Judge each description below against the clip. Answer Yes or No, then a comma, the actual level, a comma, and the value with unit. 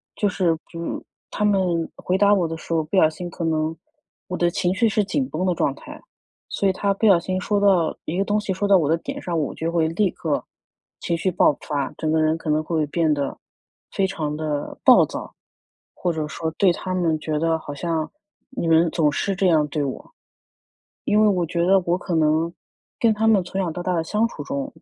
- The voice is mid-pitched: Yes, medium, 170 Hz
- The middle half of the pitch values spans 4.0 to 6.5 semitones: No, average, 3.4 semitones